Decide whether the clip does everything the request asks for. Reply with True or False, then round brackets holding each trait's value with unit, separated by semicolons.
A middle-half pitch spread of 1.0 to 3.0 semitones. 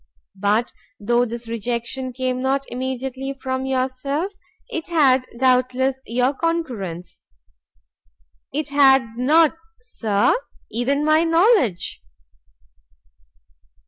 True (2.7 semitones)